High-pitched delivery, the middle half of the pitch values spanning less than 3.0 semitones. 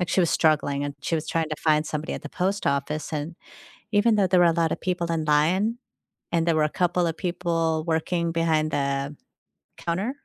No: medium, 165 Hz; narrow, 2.4 semitones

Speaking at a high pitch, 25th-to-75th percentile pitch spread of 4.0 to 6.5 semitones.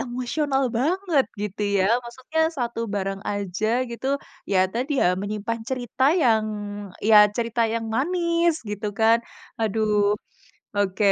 Yes: high, 230 Hz; average, 4.3 semitones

